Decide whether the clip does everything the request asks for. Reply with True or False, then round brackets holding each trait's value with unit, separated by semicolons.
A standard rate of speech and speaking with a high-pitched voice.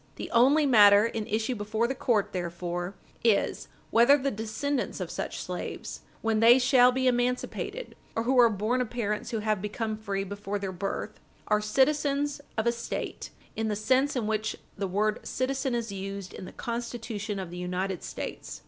True (180 wpm; 220 Hz)